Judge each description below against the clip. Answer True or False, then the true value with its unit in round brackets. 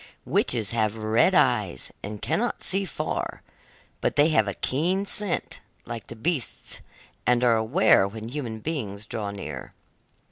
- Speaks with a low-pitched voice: True (115 Hz)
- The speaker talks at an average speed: True (145 wpm)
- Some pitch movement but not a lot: False (6.0 semitones)